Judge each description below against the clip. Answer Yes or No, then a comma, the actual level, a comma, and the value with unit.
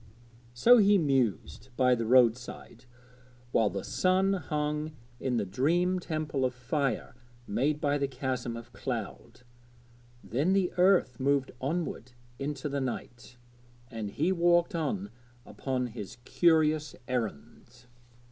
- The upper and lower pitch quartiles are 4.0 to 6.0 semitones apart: Yes, average, 4.6 semitones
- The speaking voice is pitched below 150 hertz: Yes, low, 135 Hz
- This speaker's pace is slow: Yes, slow, 130 wpm